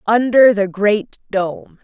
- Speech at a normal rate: No, slow, 130 wpm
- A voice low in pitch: No, high, 210 Hz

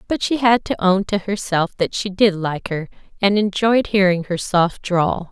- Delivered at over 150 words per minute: Yes, fast, 205 wpm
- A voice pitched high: Yes, high, 195 Hz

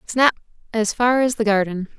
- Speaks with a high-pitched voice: Yes, high, 225 Hz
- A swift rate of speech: No, average, 180 wpm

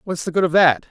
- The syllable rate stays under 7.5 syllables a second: No, 7.7 syllables/s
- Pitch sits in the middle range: Yes, medium, 165 Hz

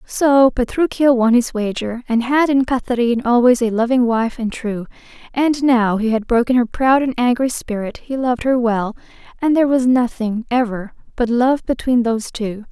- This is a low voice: No, high, 240 Hz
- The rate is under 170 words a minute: No, average, 185 wpm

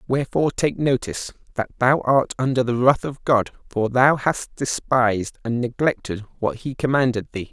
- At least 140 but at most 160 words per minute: No, average, 170 wpm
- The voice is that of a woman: No, male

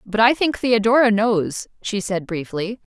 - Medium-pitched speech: No, high, 215 Hz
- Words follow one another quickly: No, average, 165 wpm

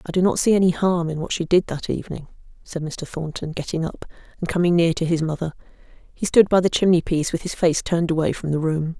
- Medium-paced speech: No, fast, 245 wpm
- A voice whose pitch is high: No, medium, 170 Hz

